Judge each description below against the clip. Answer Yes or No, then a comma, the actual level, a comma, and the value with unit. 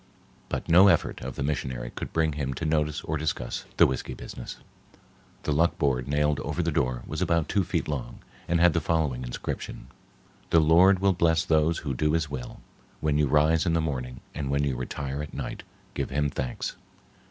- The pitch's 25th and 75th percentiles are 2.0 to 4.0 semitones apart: Yes, average, 3.1 semitones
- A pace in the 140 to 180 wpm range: No, average, 200 wpm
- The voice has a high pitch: No, very low, 75 Hz